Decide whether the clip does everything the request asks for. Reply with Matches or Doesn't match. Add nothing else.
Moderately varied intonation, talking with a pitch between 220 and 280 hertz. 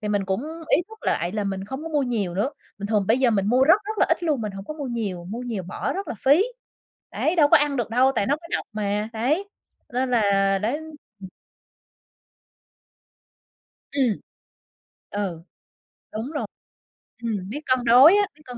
Doesn't match